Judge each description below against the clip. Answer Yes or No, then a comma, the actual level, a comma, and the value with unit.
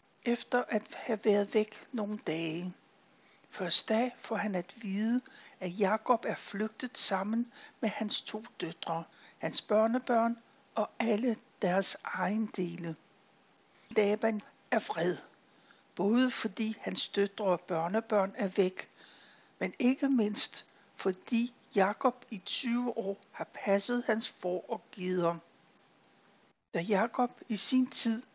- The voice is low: No, high, 215 Hz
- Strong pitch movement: No, average, 3.6 semitones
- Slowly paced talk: Yes, slow, 125 wpm